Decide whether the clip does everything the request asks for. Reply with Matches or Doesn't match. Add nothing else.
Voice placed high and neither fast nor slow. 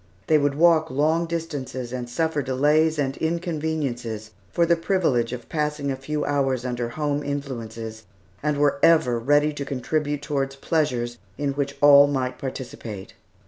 Doesn't match